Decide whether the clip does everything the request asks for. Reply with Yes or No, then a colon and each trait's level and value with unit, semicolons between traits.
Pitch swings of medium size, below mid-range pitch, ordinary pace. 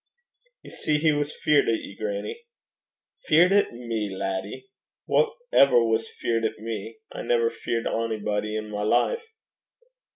No: wide, 6.2 semitones; low, 115 Hz; average, 150 wpm